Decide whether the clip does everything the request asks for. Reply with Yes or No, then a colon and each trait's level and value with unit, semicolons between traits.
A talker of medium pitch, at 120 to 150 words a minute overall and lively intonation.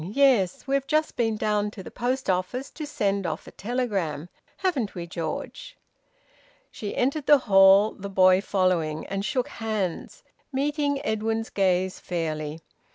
No: high, 205 Hz; average, 145 wpm; wide, 6.0 semitones